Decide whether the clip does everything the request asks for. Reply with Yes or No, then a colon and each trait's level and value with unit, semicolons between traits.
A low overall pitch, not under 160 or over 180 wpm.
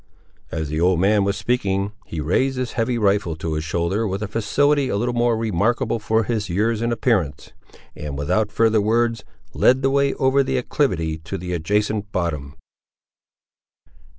Yes: low, 105 Hz; average, 165 wpm